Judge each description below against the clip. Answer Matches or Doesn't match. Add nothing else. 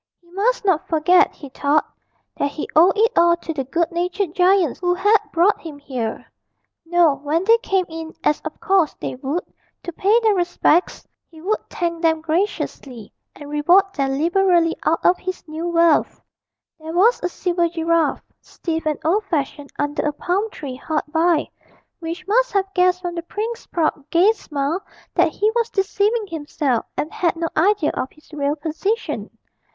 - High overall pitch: Matches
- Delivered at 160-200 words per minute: Matches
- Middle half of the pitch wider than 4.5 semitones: Doesn't match